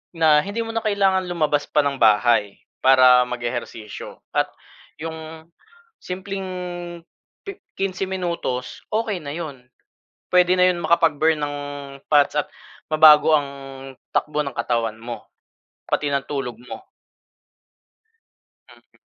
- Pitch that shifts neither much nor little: No, wide, 5.9 semitones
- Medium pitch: Yes, medium, 155 Hz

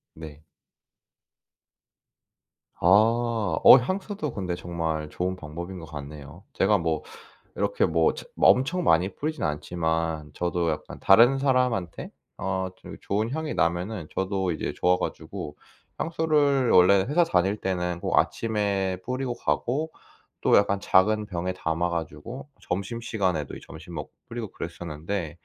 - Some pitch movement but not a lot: No, wide, 5.8 semitones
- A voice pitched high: No, very low, 95 Hz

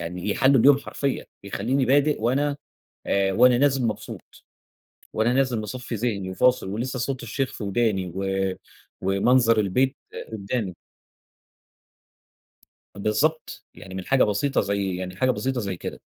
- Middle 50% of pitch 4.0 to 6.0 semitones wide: Yes, average, 5.0 semitones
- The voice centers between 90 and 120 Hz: Yes, low, 115 Hz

